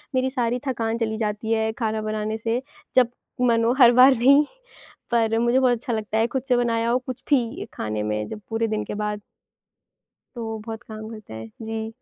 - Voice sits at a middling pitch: No, high, 225 Hz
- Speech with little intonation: Yes, narrow, 1.9 semitones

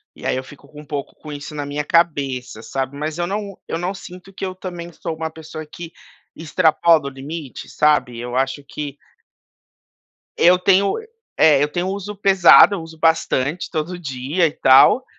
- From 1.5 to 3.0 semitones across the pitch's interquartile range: No, average, 3.8 semitones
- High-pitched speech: No, medium, 155 Hz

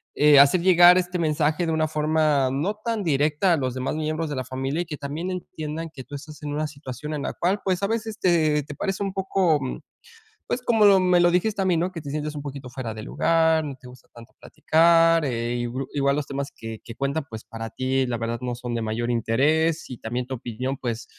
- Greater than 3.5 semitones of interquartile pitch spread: Yes, average, 4.6 semitones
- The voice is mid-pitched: Yes, medium, 150 Hz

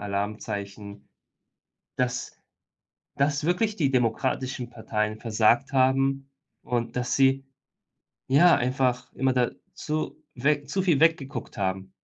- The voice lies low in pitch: Yes, low, 130 Hz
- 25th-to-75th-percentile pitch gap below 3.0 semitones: No, average, 3.9 semitones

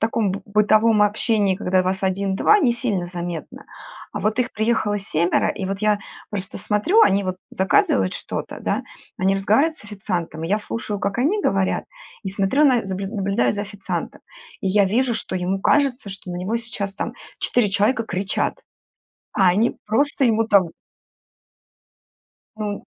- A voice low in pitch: No, high, 205 Hz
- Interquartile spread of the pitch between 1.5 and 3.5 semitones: Yes, average, 2.9 semitones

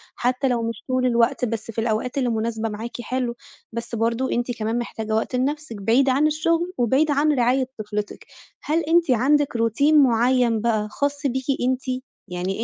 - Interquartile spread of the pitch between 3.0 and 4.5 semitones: Yes, average, 3.3 semitones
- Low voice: No, high, 245 Hz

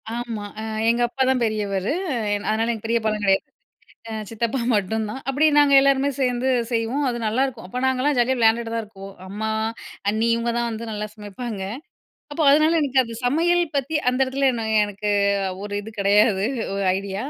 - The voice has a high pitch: Yes, high, 230 Hz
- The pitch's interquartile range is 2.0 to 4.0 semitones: Yes, average, 3.7 semitones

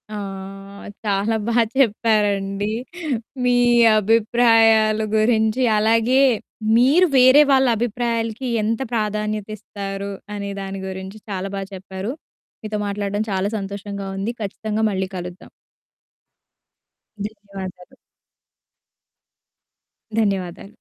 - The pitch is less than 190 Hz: No, high, 210 Hz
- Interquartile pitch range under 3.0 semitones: Yes, narrow, 2.5 semitones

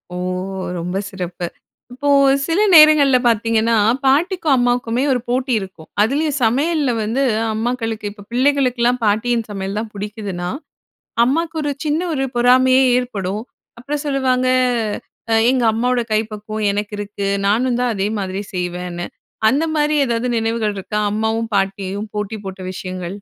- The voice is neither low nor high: No, high, 230 Hz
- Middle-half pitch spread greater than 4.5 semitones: No, average, 4.2 semitones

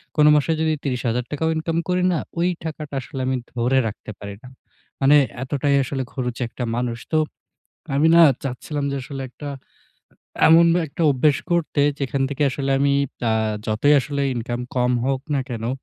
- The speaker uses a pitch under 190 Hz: Yes, medium, 140 Hz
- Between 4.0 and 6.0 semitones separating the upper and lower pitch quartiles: No, average, 3.3 semitones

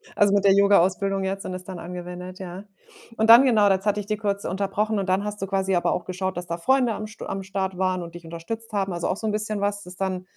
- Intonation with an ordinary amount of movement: No, narrow, 2.1 semitones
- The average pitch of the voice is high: Yes, high, 195 Hz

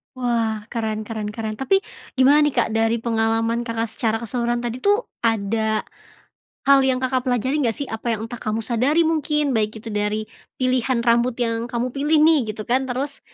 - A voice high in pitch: Yes, high, 235 Hz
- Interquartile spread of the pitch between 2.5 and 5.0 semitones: Yes, average, 2.8 semitones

